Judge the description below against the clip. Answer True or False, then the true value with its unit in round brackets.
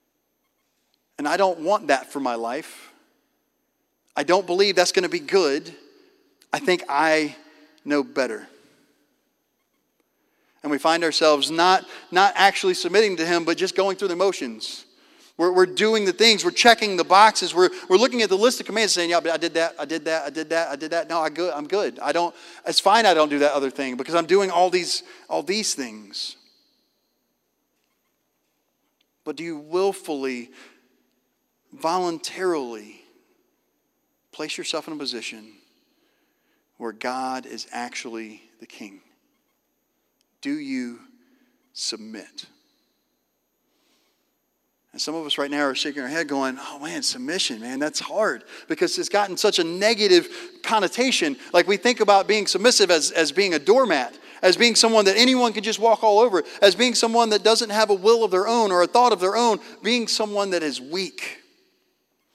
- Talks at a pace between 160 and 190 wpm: True (170 wpm)